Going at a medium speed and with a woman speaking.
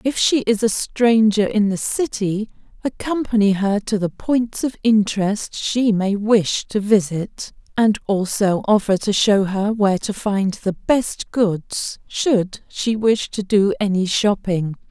Yes: average, 155 wpm; female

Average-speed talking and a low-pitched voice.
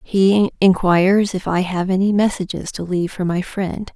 No: average, 180 wpm; high, 190 Hz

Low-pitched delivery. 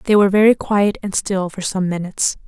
No: high, 195 Hz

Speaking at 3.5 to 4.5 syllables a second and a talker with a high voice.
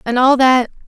No: 5.0 syllables/s; very high, 255 Hz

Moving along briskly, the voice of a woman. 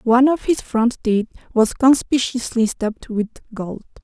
No: average, 150 wpm; female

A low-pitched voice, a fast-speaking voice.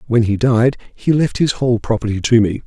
Yes: low, 120 Hz; fast, 225 wpm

